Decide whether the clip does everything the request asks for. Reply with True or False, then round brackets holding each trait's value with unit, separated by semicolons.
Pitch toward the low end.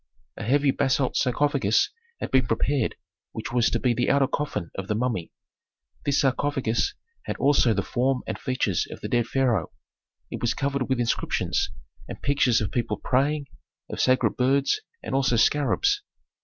True (130 Hz)